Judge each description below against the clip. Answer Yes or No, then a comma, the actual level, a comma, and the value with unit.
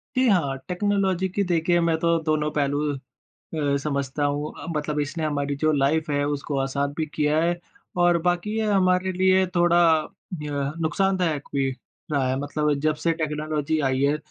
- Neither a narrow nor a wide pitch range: Yes, average, 3.4 semitones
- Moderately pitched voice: Yes, medium, 155 Hz